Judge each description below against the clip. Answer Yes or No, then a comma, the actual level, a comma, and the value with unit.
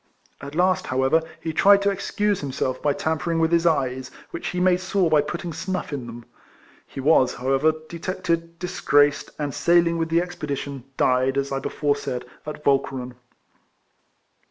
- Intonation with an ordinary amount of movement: Yes, average, 4.2 semitones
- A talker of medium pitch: Yes, medium, 155 Hz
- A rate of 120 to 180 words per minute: Yes, average, 175 wpm